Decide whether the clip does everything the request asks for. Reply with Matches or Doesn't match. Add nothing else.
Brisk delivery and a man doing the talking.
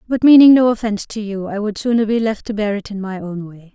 Doesn't match